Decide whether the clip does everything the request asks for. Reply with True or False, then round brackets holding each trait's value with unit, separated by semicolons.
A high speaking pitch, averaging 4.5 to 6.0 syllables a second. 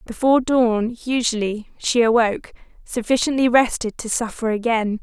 True (230 Hz; 5.0 syllables/s)